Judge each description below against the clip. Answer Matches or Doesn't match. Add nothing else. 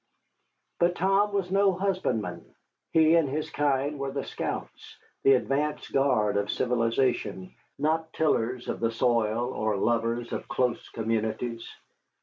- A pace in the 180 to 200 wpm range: Doesn't match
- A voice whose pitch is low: Matches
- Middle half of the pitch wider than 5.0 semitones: Matches